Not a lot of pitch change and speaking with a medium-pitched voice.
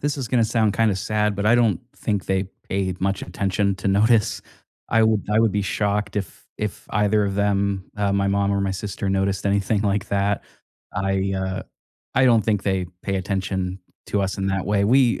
No: narrow, 1.6 semitones; low, 100 Hz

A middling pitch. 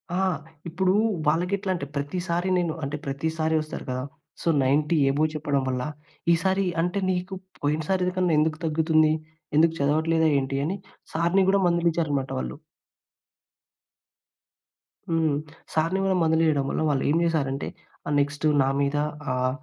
Yes: medium, 160 Hz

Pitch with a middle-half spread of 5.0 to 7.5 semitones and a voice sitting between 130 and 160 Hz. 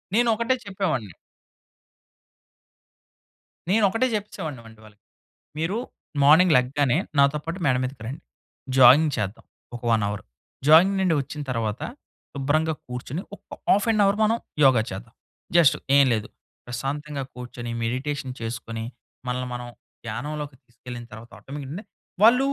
Yes: wide, 5.5 semitones; medium, 140 Hz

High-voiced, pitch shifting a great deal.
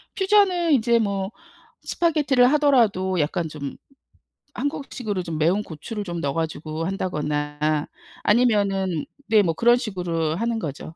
Yes: high, 195 Hz; wide, 6.9 semitones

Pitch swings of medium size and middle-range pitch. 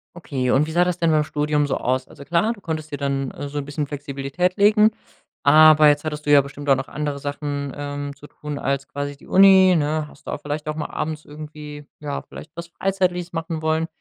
No: narrow, 2.1 semitones; medium, 150 Hz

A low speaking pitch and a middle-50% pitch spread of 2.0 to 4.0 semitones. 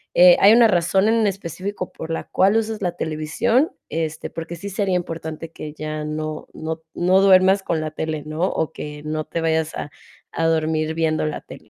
No: medium, 165 Hz; average, 3.5 semitones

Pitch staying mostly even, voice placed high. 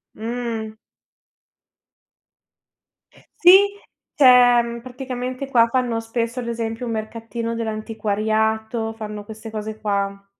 Yes: narrow, 1.5 semitones; high, 225 Hz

